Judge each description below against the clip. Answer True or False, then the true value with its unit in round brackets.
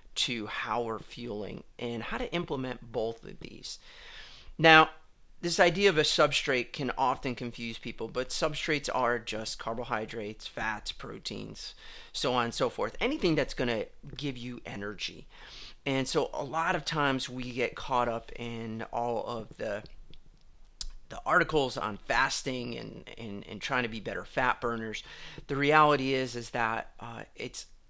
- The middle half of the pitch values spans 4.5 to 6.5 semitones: True (4.8 semitones)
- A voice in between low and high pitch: False (125 Hz)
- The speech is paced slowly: False (160 wpm)